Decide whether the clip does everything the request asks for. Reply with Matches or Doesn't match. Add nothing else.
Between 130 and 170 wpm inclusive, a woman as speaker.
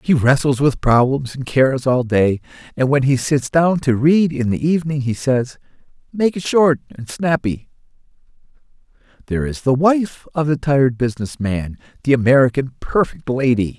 Doesn't match